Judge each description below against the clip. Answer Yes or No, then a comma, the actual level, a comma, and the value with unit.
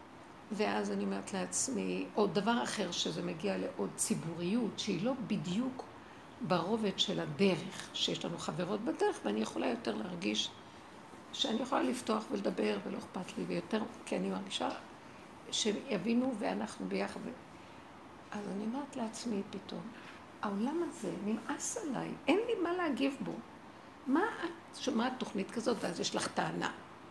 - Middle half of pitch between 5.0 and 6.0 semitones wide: Yes, average, 5.3 semitones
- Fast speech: No, average, 135 wpm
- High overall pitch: Yes, high, 220 Hz